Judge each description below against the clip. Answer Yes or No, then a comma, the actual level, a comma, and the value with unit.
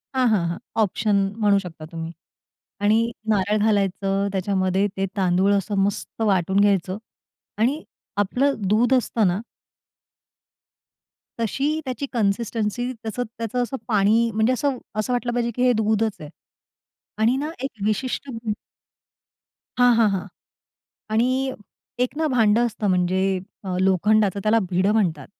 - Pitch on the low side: No, high, 215 Hz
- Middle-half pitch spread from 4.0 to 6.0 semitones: No, average, 3.4 semitones